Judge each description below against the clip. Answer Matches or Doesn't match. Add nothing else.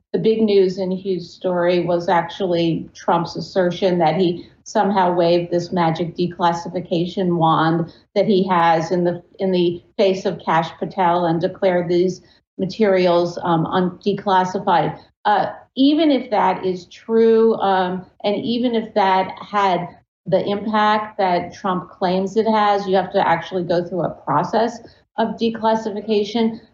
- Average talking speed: Matches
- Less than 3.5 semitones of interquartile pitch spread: Matches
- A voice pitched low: Doesn't match